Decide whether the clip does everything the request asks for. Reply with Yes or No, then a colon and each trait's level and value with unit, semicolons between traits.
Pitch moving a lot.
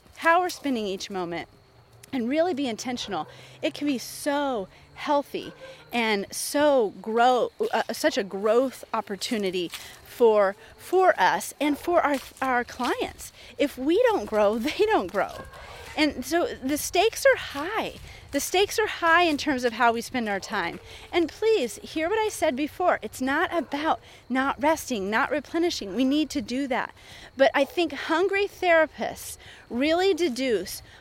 Yes: wide, 6.3 semitones